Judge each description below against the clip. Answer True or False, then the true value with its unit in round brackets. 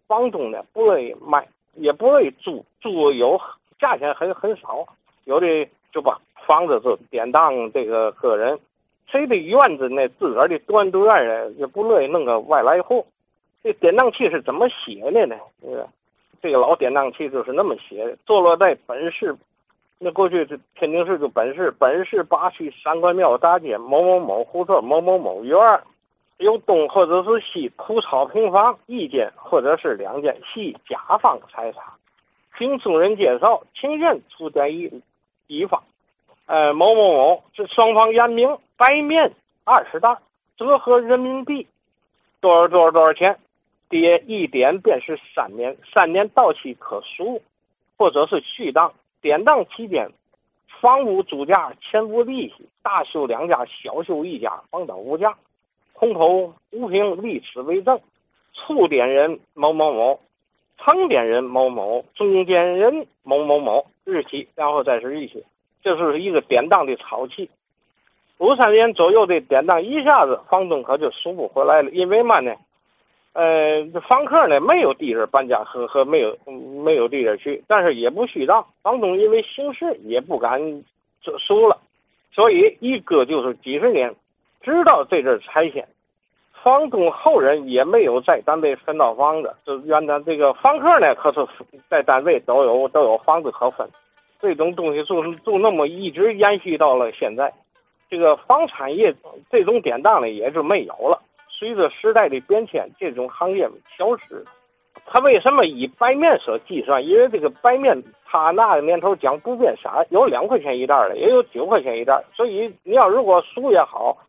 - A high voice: True (225 Hz)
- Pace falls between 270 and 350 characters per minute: False (240 characters per minute)